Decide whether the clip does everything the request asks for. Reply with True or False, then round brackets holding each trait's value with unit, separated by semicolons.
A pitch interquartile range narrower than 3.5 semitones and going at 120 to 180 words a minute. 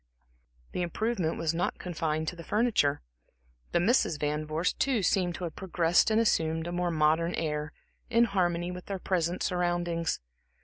True (2.4 semitones; 165 wpm)